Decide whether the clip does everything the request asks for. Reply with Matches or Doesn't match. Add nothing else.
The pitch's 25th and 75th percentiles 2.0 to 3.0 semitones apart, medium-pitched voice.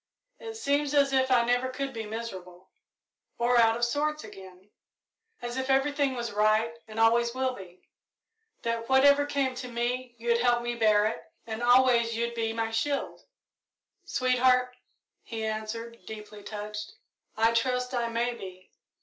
Doesn't match